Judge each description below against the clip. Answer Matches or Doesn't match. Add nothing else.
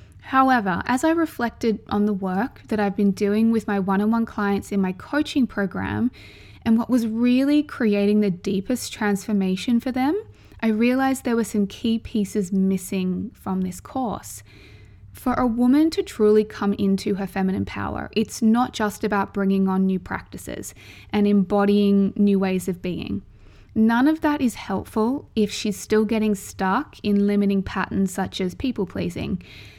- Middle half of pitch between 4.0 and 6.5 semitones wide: Doesn't match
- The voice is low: Doesn't match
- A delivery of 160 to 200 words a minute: Matches